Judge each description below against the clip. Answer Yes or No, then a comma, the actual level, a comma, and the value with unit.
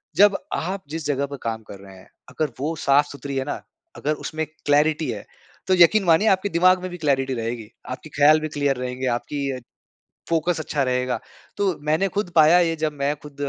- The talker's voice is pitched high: No, medium, 150 Hz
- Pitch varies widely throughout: No, average, 3.7 semitones